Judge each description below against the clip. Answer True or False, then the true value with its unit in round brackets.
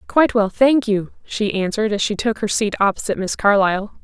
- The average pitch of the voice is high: True (210 Hz)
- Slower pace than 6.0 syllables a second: False (6.1 syllables/s)